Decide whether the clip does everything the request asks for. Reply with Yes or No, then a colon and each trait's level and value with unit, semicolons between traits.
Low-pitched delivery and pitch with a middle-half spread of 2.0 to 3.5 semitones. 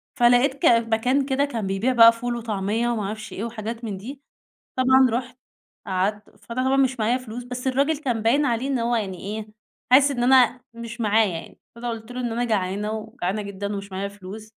No: high, 230 Hz; average, 3.0 semitones